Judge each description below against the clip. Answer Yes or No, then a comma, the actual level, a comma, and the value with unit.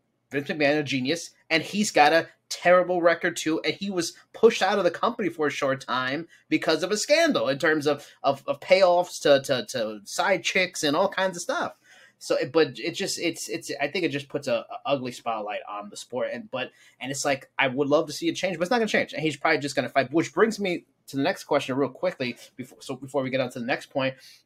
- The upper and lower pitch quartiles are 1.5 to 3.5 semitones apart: No, average, 4.5 semitones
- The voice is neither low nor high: Yes, medium, 160 Hz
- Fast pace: Yes, fast, 255 wpm